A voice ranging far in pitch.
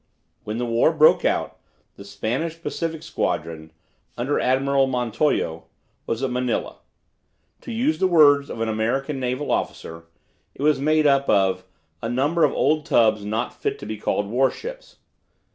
Yes: wide, 5.7 semitones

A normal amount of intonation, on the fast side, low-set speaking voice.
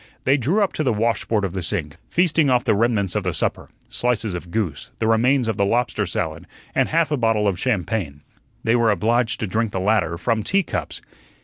Yes: average, 3.8 semitones; fast, 210 wpm; low, 110 Hz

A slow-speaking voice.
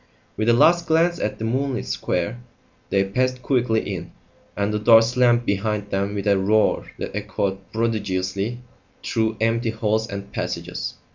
No: average, 155 wpm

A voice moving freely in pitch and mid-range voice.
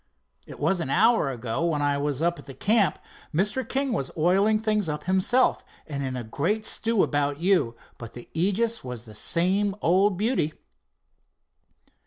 Yes: wide, 6.7 semitones; medium, 175 Hz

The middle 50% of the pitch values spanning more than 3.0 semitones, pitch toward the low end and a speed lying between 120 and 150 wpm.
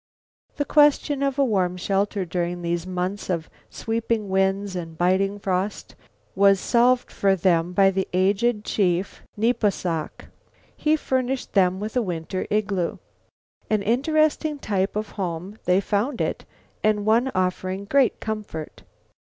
No: average, 3.8 semitones; high, 200 Hz; average, 140 wpm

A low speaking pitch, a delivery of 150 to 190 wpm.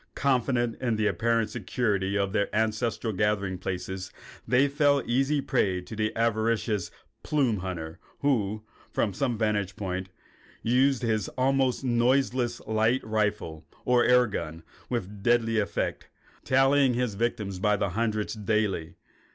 No: low, 110 Hz; slow, 135 wpm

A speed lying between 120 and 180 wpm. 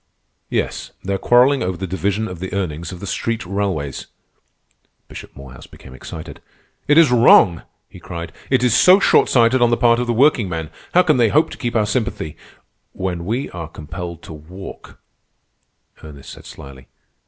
Yes: average, 175 wpm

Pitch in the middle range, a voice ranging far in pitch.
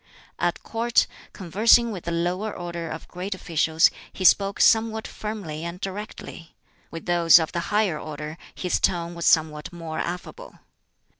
No: medium, 175 Hz; average, 3.7 semitones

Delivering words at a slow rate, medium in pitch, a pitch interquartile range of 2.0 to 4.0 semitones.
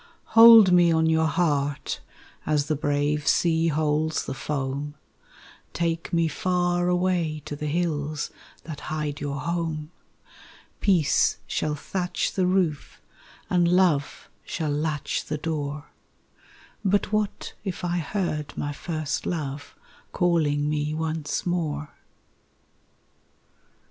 Yes: slow, 120 wpm; medium, 155 Hz; average, 3.0 semitones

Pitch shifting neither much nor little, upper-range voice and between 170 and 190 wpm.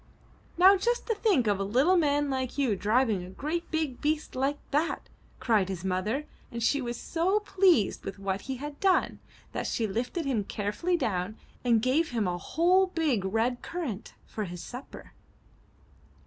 No: wide, 7.5 semitones; very high, 260 Hz; average, 175 wpm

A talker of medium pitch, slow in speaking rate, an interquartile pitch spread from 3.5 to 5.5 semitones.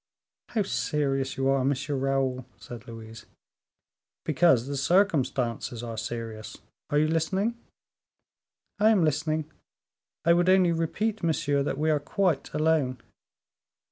Yes: medium, 145 Hz; slow, 125 wpm; average, 4.5 semitones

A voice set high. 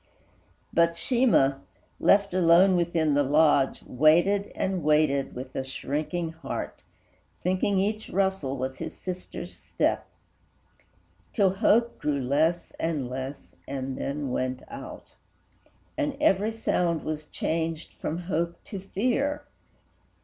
No: medium, 165 Hz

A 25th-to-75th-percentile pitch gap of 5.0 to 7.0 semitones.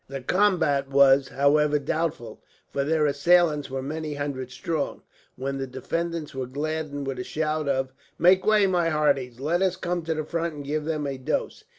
No: average, 3.2 semitones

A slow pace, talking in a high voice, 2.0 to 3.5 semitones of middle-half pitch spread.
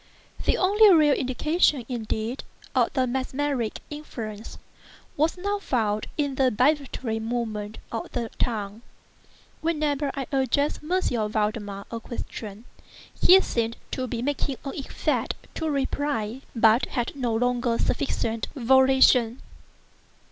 No: slow, 120 wpm; very high, 250 Hz; average, 4.2 semitones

